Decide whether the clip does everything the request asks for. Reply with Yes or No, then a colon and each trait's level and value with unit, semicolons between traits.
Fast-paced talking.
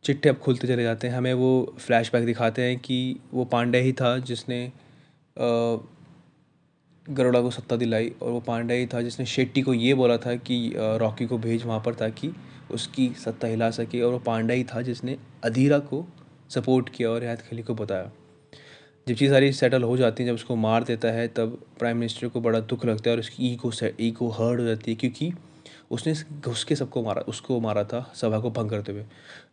Yes: fast, 205 wpm